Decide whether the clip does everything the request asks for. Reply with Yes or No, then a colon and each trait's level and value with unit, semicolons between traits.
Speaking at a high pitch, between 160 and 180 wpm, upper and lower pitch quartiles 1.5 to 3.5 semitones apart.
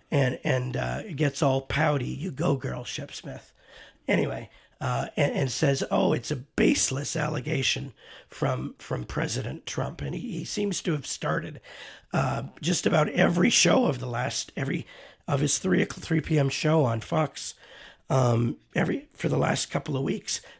No: medium, 140 Hz; average, 165 wpm; average, 2.7 semitones